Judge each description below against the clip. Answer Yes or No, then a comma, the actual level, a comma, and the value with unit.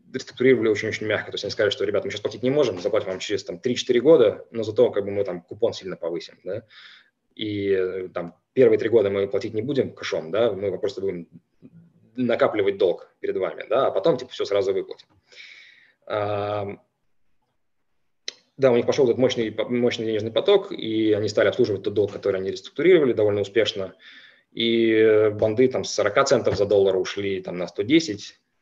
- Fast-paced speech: Yes, fast, 185 wpm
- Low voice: No, very high, 335 Hz